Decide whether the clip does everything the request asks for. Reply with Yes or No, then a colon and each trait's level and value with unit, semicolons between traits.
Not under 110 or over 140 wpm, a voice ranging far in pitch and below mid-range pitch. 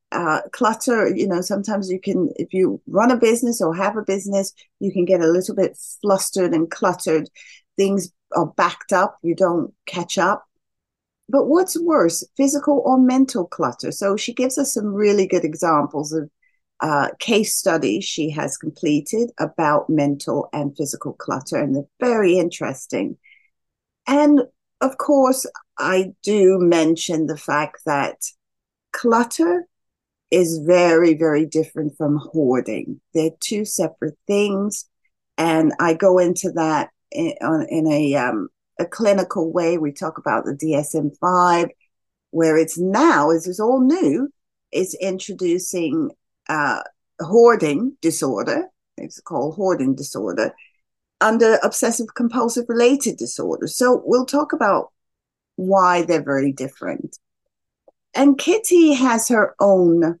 No: slow, 135 wpm; wide, 7.0 semitones; high, 190 Hz